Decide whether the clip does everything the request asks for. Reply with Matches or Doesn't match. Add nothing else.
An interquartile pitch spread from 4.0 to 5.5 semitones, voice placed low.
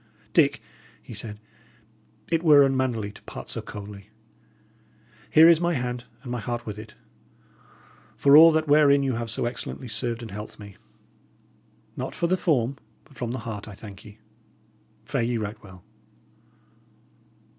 Matches